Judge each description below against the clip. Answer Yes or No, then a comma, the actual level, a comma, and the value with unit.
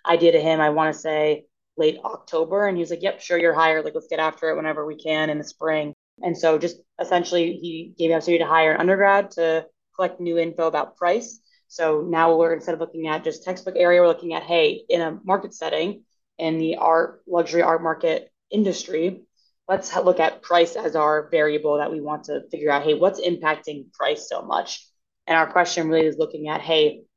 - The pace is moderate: No, fast, 215 wpm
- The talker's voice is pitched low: No, medium, 165 Hz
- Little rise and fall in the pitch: Yes, narrow, 2.1 semitones